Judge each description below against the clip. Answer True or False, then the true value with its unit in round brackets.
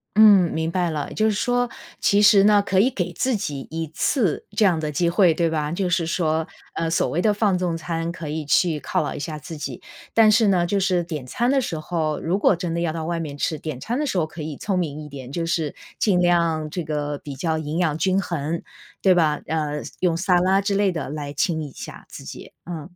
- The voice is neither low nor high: True (170 Hz)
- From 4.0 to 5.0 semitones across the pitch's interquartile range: False (3.4 semitones)